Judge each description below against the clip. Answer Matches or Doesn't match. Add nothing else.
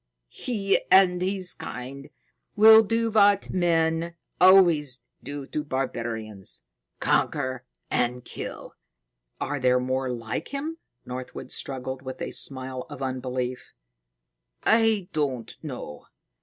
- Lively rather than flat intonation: Matches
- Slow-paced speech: Matches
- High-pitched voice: Doesn't match